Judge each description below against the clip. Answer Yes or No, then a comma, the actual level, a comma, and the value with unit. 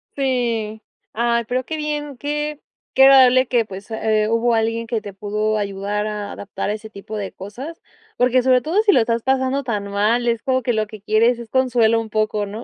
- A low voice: No, high, 230 Hz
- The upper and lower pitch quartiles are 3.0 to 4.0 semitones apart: Yes, average, 3.3 semitones